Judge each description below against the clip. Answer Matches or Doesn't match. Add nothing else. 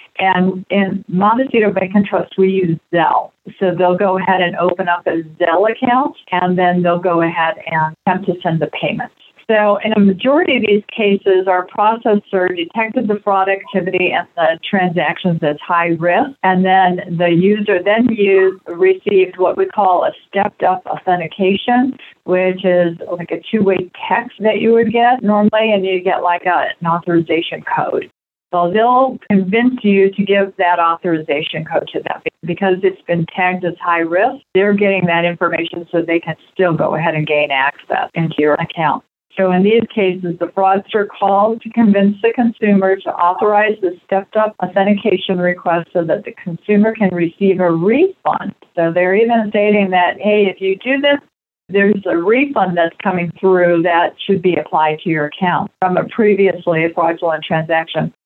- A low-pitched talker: Doesn't match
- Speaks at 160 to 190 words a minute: Matches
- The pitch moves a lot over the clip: Doesn't match